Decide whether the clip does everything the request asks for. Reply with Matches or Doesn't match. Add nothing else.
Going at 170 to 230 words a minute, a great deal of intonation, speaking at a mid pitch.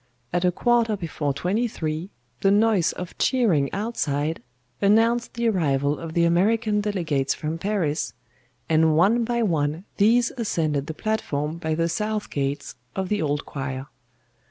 Doesn't match